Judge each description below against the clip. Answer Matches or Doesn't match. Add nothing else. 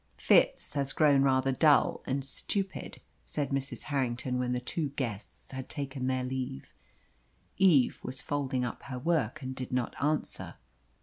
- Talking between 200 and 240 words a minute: Doesn't match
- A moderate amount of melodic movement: Doesn't match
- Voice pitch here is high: Doesn't match